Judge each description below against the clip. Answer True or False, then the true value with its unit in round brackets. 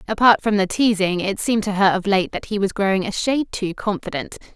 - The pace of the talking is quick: True (235 wpm)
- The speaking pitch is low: False (200 Hz)